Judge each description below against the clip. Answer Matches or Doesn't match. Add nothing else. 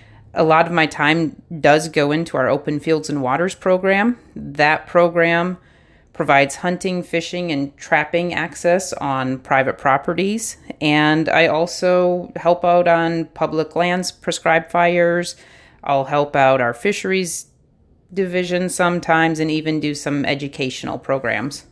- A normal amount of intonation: Matches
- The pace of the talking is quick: Doesn't match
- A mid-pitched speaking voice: Matches